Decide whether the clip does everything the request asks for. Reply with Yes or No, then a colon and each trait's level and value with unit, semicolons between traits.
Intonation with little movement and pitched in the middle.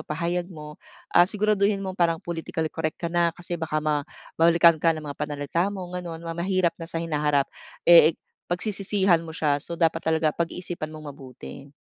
Yes: narrow, 2.2 semitones; medium, 165 Hz